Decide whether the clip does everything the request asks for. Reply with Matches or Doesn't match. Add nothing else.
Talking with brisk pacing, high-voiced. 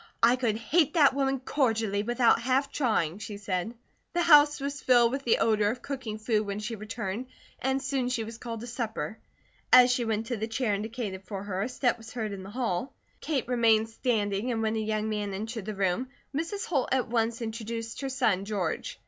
Matches